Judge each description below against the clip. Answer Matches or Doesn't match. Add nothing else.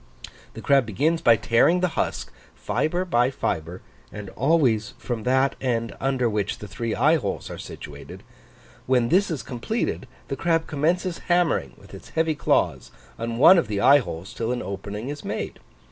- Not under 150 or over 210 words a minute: Matches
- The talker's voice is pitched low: Matches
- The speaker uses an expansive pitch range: Matches